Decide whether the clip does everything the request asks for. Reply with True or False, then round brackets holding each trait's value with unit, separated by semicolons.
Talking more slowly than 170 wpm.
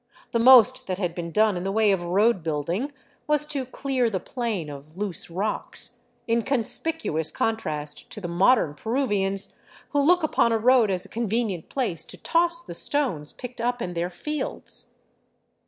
False (175 wpm)